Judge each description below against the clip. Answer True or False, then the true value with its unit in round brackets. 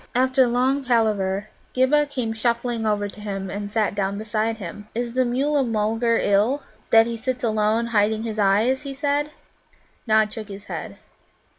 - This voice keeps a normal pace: True (165 wpm)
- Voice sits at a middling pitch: False (225 Hz)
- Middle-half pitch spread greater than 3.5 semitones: False (3.2 semitones)